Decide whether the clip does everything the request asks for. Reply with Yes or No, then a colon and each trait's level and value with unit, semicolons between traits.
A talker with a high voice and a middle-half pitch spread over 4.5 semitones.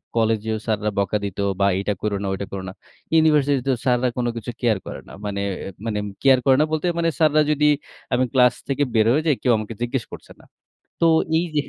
No: low, 125 Hz; average, 5.1 semitones